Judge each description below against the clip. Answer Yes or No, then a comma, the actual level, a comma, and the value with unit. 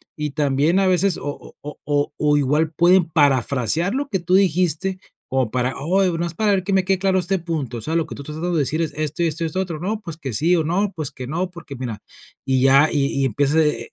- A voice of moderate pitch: Yes, medium, 160 Hz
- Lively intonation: No, average, 4.1 semitones